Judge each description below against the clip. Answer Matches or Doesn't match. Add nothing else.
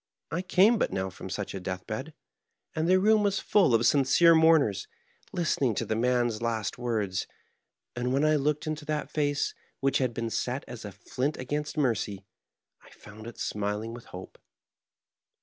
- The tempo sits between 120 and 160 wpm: Doesn't match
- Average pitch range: Doesn't match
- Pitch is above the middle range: Doesn't match